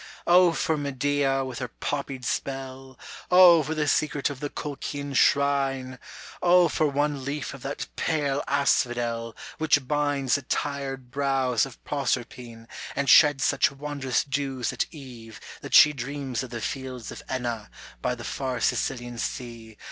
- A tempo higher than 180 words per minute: No, average, 150 wpm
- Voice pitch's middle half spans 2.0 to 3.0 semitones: Yes, narrow, 2.4 semitones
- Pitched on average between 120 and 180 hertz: Yes, low, 135 Hz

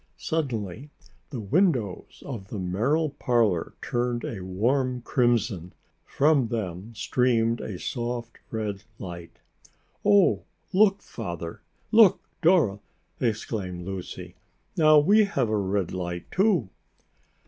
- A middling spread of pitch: No, wide, 6.5 semitones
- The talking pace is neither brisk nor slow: No, slow, 110 wpm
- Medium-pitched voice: No, low, 115 Hz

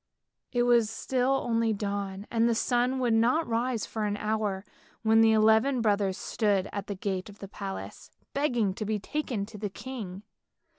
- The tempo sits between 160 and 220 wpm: Yes, average, 180 wpm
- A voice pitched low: No, high, 220 Hz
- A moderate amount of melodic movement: Yes, average, 3.0 semitones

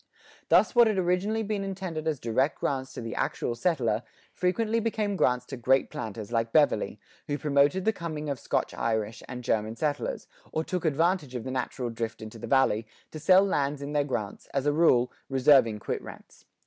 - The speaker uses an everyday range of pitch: No, wide, 6.6 semitones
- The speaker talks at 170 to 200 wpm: Yes, average, 190 wpm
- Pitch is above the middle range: No, medium, 140 Hz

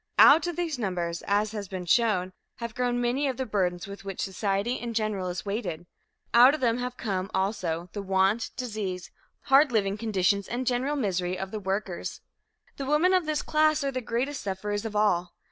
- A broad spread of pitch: No, average, 4.7 semitones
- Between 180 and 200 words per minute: Yes, average, 195 wpm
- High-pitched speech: Yes, high, 215 Hz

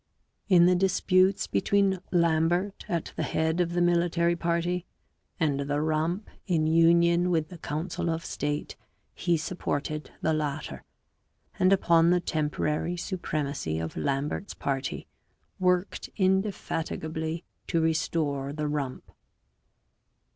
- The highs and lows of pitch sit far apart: No, narrow, 2.6 semitones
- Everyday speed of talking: No, slow, 120 wpm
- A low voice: No, medium, 165 Hz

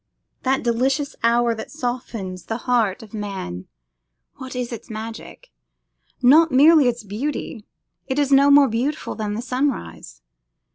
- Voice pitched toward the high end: Yes, high, 240 Hz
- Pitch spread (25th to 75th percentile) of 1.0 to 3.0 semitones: No, average, 3.9 semitones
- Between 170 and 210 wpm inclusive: No, average, 140 wpm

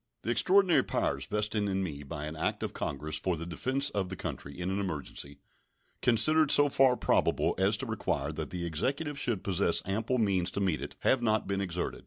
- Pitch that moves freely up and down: Yes, wide, 6.4 semitones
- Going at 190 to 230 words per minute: Yes, fast, 205 wpm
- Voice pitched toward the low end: Yes, very low, 95 Hz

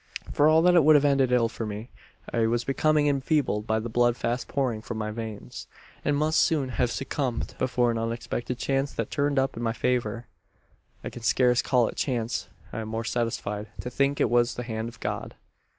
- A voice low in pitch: Yes, low, 120 Hz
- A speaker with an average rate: No, fast, 215 wpm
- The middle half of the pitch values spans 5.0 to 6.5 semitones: No, average, 3.2 semitones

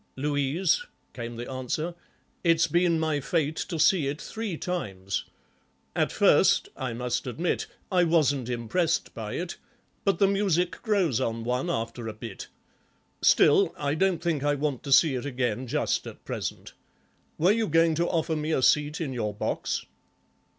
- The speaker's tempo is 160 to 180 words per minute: Yes, average, 165 wpm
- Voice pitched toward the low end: No, medium, 150 Hz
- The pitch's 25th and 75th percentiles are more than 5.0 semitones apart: Yes, wide, 5.4 semitones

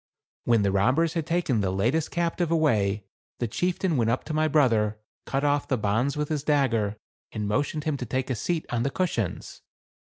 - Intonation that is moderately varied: No, wide, 6.3 semitones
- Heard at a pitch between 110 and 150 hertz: Yes, low, 135 Hz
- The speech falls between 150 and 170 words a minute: No, average, 195 wpm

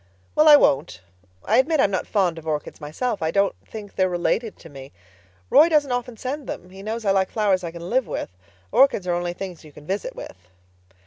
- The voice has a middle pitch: No, high, 195 Hz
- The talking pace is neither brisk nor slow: No, fast, 210 wpm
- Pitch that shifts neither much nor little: No, wide, 5.9 semitones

